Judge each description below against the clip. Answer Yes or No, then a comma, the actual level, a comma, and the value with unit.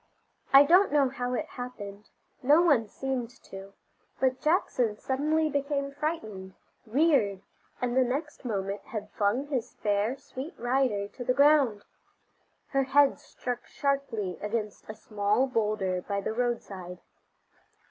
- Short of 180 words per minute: Yes, slow, 135 wpm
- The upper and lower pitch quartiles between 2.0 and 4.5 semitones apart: No, average, 5.1 semitones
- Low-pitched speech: No, very high, 250 Hz